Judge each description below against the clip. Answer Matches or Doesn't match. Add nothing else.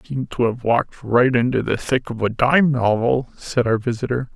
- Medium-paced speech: Doesn't match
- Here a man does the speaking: Matches